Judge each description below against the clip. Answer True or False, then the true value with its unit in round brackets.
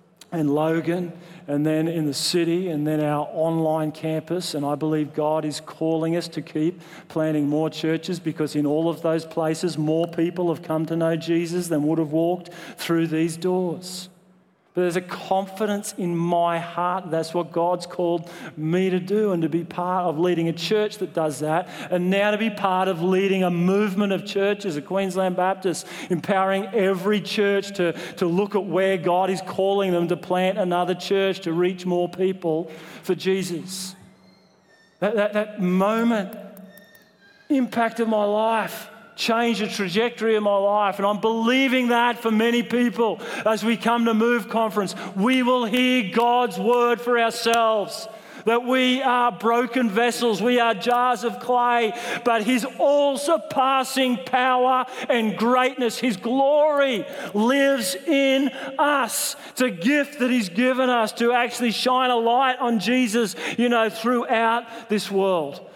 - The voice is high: True (200 Hz)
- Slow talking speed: False (165 wpm)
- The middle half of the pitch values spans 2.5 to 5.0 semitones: False (5.4 semitones)